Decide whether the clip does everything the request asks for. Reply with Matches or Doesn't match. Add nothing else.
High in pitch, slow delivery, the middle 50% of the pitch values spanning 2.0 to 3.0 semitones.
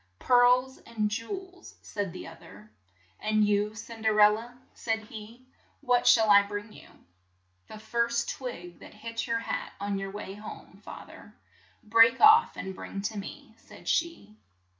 Doesn't match